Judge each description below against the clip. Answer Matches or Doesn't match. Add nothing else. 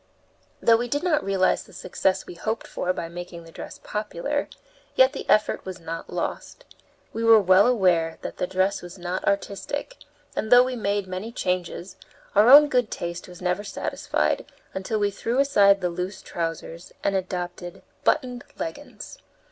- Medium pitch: Doesn't match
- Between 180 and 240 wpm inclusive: Doesn't match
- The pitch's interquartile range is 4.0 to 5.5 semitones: Matches